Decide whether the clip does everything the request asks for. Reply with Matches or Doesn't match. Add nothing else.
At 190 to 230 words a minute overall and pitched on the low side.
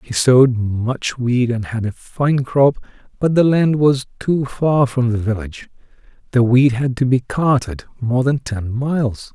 Doesn't match